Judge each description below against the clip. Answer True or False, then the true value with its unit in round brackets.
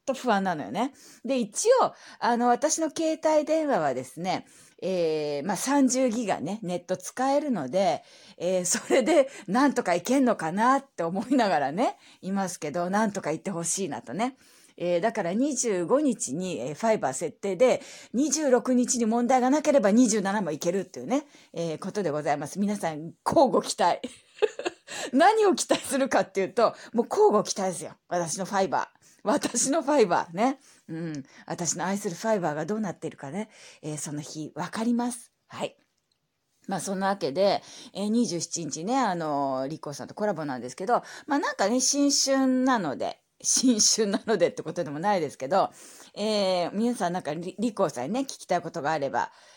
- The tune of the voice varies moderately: False (6.9 semitones)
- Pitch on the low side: False (215 Hz)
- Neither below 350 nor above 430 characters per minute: False (340 characters per minute)